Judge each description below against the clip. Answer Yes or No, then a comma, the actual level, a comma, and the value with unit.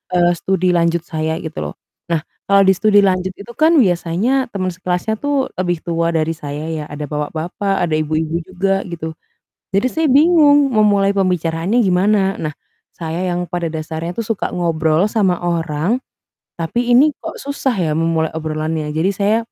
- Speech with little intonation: No, average, 4.0 semitones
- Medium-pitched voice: Yes, medium, 180 Hz